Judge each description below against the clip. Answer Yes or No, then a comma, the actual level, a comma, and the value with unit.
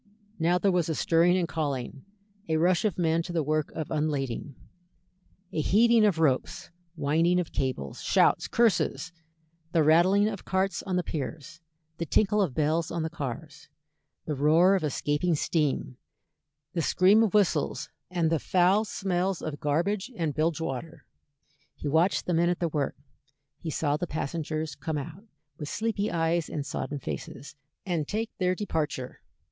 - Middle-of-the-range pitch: Yes, medium, 165 Hz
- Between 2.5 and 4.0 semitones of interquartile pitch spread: Yes, average, 3.4 semitones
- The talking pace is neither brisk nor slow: Yes, average, 165 wpm